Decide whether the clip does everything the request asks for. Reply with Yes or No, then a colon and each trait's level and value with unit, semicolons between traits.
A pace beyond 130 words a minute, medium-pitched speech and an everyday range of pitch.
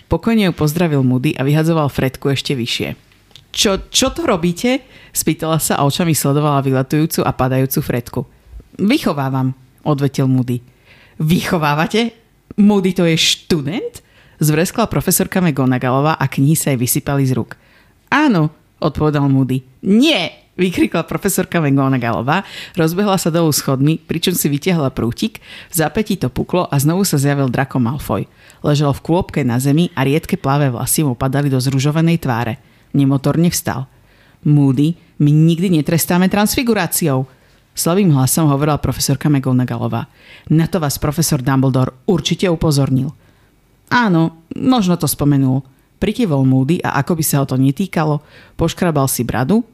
Yes: average, 140 wpm; medium, 150 Hz; average, 4.4 semitones